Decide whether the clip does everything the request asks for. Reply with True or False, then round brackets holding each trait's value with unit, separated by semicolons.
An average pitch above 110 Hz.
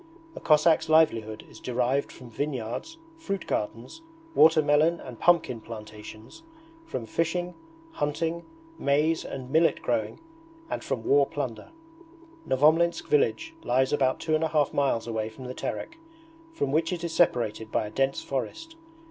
True (140 Hz)